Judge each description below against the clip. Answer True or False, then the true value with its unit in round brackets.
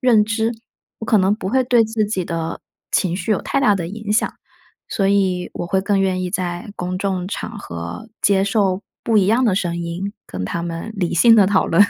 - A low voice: False (195 Hz)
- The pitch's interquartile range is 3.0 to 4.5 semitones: True (3.4 semitones)